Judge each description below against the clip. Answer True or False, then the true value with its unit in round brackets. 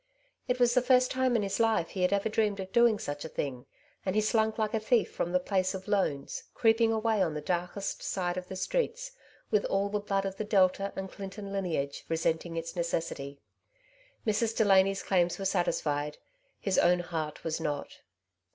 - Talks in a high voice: True (195 Hz)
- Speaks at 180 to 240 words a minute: True (195 wpm)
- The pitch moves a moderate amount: True (3.9 semitones)